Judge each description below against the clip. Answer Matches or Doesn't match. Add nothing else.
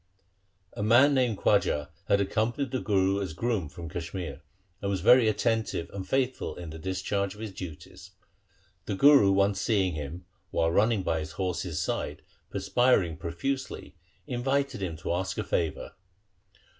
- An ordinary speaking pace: Matches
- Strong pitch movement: Doesn't match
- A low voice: Matches